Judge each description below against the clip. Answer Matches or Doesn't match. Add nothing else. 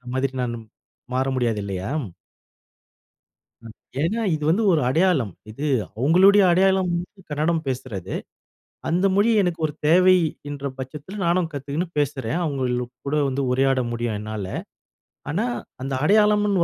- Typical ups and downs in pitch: Doesn't match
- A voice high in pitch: Doesn't match